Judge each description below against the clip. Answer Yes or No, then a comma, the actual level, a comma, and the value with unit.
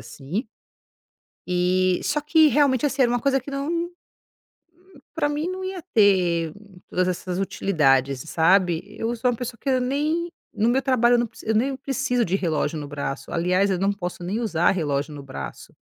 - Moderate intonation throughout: No, wide, 7.7 semitones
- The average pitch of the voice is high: Yes, high, 210 Hz